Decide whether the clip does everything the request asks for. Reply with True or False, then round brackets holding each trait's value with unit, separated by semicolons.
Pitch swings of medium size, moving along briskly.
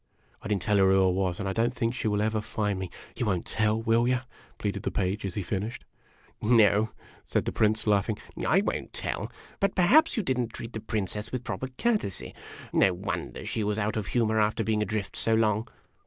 False (2.2 semitones; 230 wpm)